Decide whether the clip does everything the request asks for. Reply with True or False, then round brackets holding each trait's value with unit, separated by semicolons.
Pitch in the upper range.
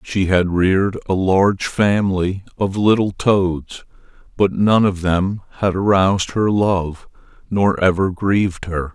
False (95 Hz)